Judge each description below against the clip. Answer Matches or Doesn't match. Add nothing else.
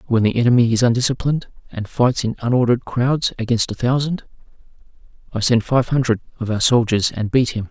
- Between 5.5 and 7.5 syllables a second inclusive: Matches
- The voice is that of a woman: Doesn't match